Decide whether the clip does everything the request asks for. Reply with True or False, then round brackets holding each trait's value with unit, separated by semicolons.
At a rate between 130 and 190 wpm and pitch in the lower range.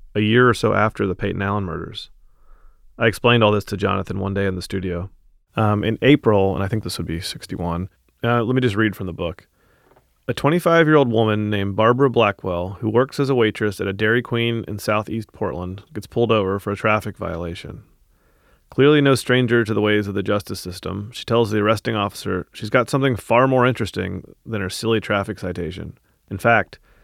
False (205 wpm; 105 Hz)